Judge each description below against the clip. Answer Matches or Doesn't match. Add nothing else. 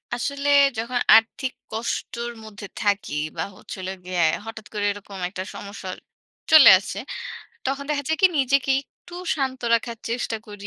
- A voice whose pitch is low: Doesn't match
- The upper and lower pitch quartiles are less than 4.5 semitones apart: Doesn't match